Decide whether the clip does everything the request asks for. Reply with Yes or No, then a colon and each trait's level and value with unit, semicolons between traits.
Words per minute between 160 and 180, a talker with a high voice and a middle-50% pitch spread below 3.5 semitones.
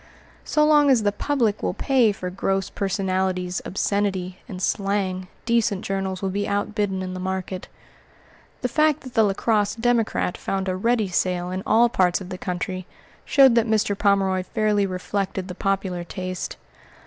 Yes: average, 165 wpm; high, 195 Hz; average, 2.7 semitones